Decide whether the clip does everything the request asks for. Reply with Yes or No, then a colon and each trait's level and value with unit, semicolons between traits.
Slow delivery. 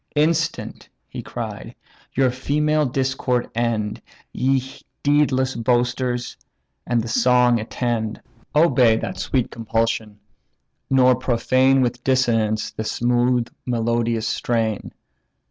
Yes: slow, 100 wpm